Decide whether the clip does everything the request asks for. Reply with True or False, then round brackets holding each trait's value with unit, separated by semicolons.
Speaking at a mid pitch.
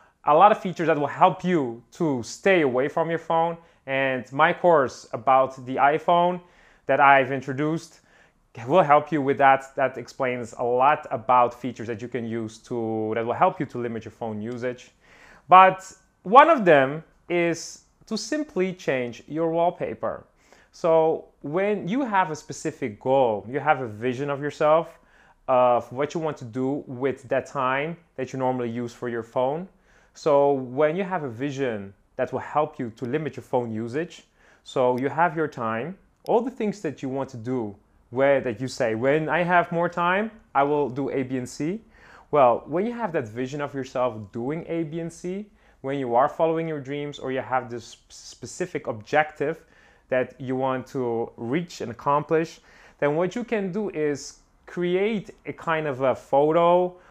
True (145 Hz)